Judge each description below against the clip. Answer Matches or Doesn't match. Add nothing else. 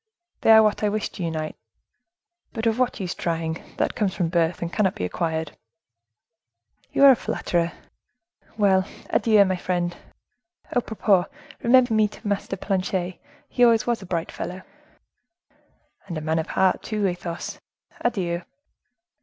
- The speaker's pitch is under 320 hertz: Matches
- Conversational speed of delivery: Matches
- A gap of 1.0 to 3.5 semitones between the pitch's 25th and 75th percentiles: Doesn't match